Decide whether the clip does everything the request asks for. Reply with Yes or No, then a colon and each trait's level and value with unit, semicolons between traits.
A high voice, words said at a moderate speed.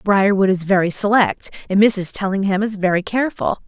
Yes: high, 200 Hz; average, 165 wpm